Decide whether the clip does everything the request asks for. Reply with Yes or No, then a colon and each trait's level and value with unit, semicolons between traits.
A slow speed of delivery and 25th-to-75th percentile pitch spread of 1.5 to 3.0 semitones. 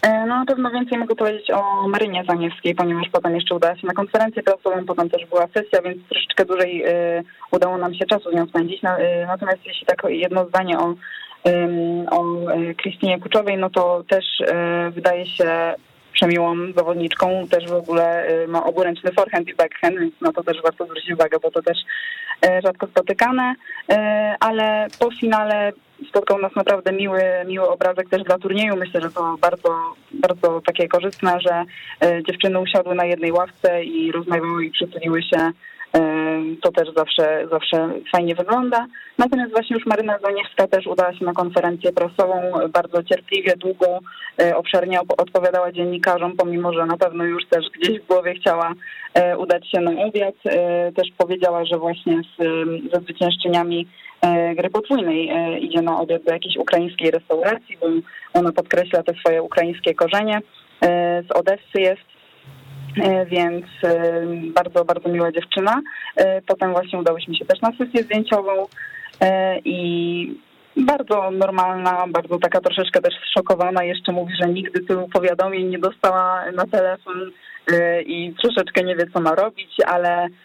No: average, 150 wpm; narrow, 2.4 semitones